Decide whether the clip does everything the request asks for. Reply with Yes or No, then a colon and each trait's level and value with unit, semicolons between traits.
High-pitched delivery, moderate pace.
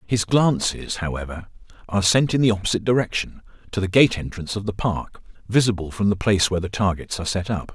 No: low, 100 Hz; average, 195 wpm